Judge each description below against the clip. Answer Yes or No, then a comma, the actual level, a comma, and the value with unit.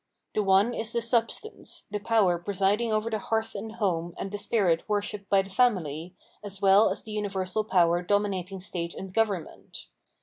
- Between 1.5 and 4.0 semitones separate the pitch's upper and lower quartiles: Yes, average, 2.8 semitones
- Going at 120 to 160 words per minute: No, average, 175 wpm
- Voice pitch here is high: Yes, high, 200 Hz